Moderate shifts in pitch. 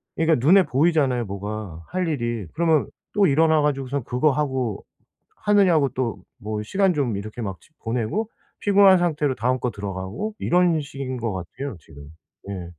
No: wide, 7.0 semitones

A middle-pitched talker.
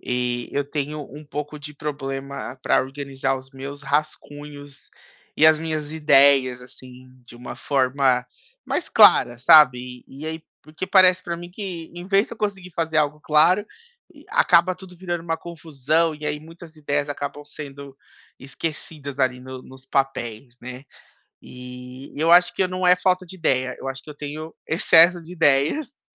Yes: medium, 145 Hz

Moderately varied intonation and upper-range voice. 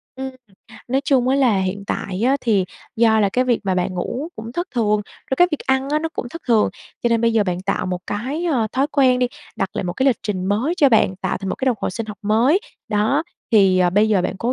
Yes: average, 4.8 semitones; high, 230 Hz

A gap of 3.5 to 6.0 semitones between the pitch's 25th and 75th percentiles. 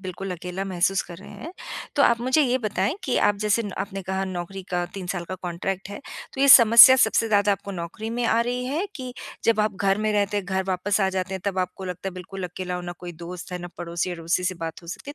No: average, 3.0 semitones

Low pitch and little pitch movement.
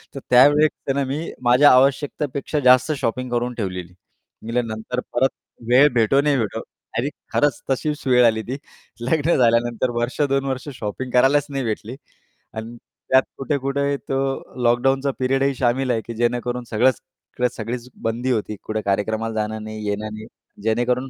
No: low, 125 Hz; average, 3.1 semitones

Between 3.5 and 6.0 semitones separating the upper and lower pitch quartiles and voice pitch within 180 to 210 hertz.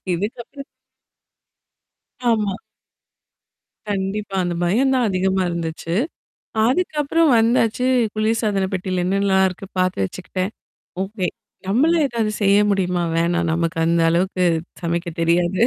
Yes: average, 4.1 semitones; high, 190 Hz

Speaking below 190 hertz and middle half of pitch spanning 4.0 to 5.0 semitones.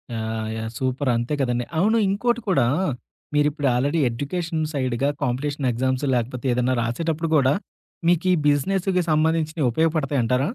Yes: medium, 140 Hz; average, 4.6 semitones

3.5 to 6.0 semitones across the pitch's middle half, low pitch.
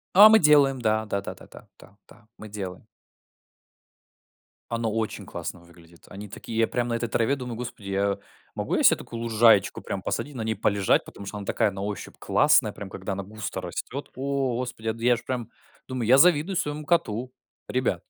Yes: average, 4.0 semitones; low, 115 Hz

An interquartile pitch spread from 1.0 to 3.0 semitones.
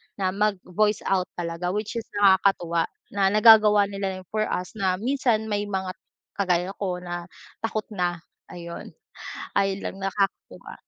Yes: narrow, 2.5 semitones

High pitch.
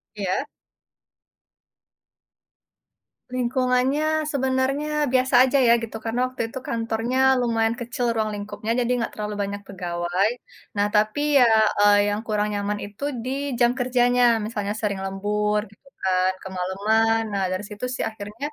Yes: high, 220 Hz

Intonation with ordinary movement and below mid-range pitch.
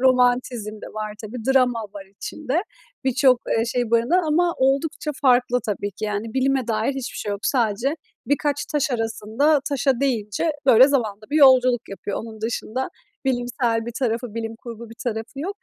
No: average, 3.2 semitones; high, 245 Hz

